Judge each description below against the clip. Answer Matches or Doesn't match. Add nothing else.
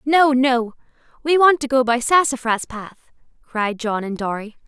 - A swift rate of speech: Doesn't match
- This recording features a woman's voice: Matches